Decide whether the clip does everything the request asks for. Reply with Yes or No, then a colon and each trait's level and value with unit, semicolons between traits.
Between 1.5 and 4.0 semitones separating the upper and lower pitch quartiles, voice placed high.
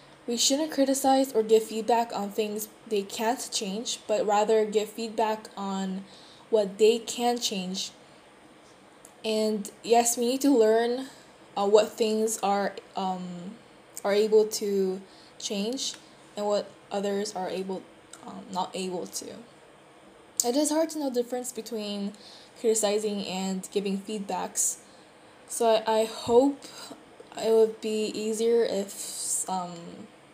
Yes: average, 2.7 semitones; high, 220 Hz